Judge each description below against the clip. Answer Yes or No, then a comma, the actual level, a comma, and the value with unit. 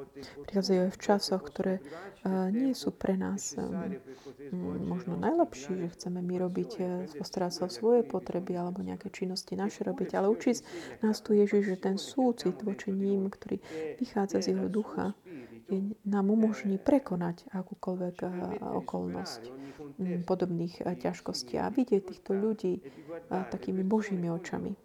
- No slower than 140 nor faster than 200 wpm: No, average, 130 wpm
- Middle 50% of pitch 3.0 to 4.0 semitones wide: No, narrow, 2.6 semitones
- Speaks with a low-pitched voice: No, high, 190 Hz